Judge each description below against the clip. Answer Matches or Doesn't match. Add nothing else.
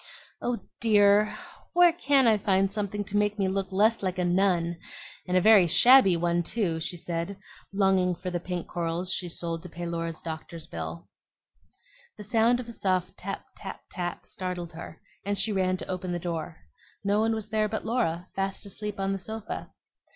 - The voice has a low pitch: Doesn't match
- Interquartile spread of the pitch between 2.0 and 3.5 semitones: Matches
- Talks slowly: Doesn't match